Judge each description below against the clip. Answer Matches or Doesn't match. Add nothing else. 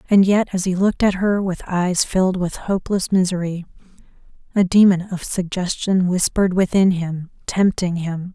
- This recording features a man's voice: Doesn't match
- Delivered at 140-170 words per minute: Matches